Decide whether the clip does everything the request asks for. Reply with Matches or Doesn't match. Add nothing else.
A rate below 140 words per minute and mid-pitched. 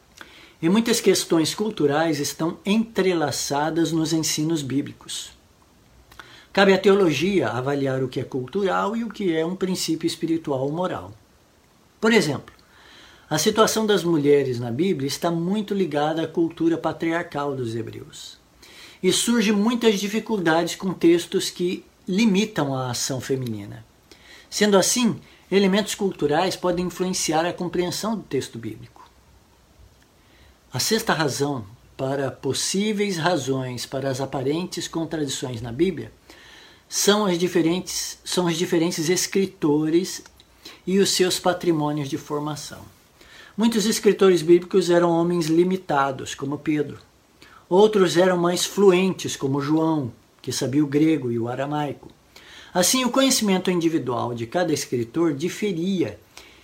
Matches